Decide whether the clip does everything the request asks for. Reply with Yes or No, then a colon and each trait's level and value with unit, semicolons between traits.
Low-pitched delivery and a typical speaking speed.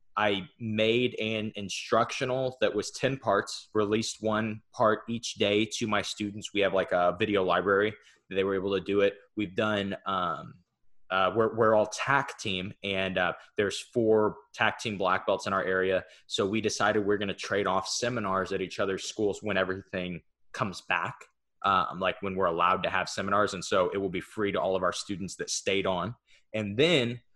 Yes: low, 105 Hz; average, 195 wpm